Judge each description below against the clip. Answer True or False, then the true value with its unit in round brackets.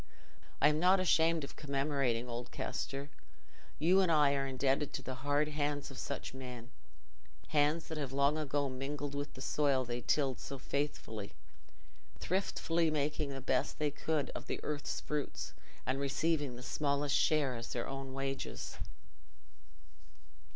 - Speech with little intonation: True (2.0 semitones)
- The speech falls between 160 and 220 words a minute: False (150 wpm)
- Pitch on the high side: False (140 Hz)